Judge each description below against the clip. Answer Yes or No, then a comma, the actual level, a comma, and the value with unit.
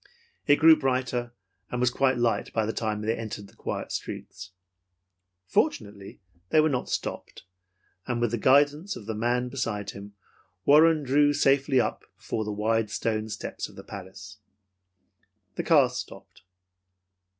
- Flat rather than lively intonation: No, average, 4.3 semitones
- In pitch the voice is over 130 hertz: No, low, 120 Hz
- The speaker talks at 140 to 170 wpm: Yes, average, 145 wpm